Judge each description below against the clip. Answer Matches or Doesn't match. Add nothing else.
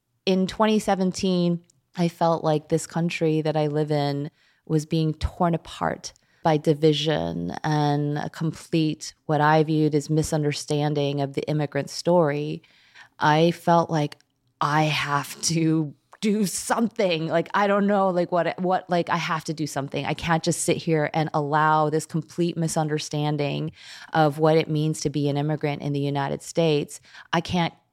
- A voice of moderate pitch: Matches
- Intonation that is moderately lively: Doesn't match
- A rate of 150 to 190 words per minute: Matches